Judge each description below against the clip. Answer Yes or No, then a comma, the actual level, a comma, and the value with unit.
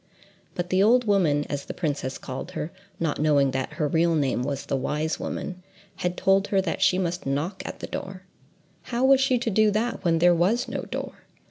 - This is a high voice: No, medium, 175 Hz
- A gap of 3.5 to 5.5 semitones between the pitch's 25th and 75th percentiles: Yes, average, 5.1 semitones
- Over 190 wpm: Yes, average, 200 wpm